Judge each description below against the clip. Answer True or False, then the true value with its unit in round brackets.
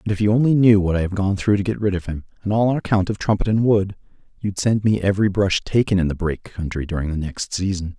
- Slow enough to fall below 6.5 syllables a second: False (6.6 syllables/s)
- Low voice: True (100 Hz)